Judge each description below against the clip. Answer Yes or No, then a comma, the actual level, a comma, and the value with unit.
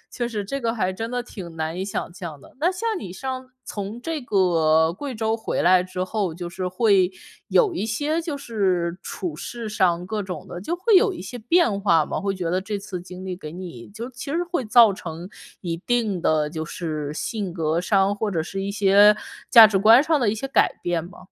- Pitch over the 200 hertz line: No, high, 195 Hz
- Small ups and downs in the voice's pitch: No, average, 5.0 semitones